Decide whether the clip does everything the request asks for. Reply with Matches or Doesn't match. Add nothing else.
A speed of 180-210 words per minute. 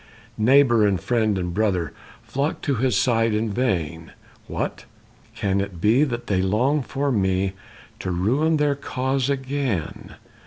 Doesn't match